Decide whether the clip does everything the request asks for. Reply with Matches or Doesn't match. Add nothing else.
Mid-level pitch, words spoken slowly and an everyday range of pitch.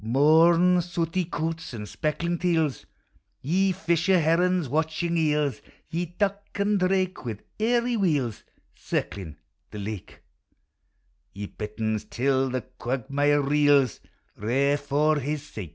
Matches